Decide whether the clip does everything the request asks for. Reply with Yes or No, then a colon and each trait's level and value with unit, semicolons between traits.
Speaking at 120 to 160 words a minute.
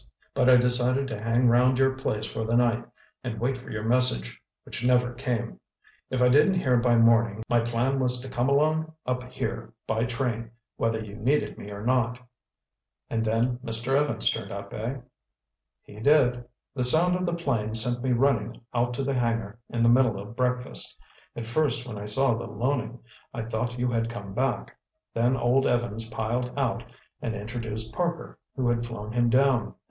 No: average, 185 wpm